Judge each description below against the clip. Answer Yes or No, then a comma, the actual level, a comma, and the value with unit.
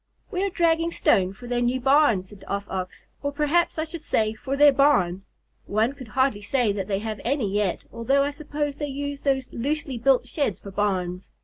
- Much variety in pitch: Yes, wide, 5.8 semitones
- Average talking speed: No, fast, 210 wpm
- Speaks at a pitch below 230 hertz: No, very high, 260 Hz